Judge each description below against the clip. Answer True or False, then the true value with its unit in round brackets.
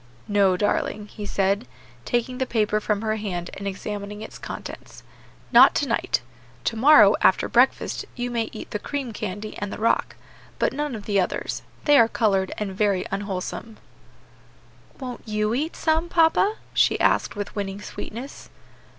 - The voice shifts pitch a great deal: False (3.2 semitones)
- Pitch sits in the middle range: False (215 Hz)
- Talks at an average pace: True (160 wpm)